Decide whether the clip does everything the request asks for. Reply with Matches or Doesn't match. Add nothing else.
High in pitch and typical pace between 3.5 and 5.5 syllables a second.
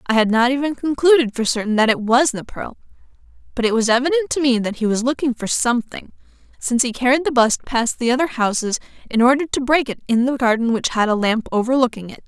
Doesn't match